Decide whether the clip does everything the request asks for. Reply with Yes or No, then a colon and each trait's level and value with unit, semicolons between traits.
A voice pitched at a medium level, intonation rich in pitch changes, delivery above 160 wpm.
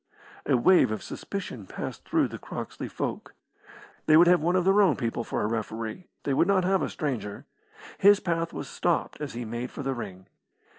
Yes: medium, 145 Hz; wide, 7.7 semitones; average, 200 wpm